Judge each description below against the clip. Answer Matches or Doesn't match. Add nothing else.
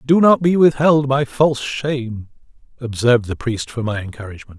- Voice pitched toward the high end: Doesn't match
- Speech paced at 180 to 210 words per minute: Doesn't match